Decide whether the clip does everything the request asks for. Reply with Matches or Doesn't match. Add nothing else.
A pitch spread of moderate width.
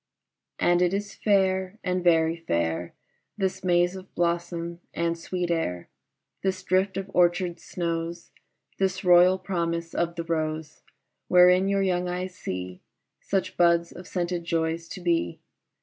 Doesn't match